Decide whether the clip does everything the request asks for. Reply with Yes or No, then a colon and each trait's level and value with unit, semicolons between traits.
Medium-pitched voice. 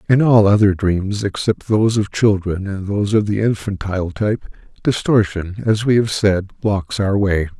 No: low, 100 Hz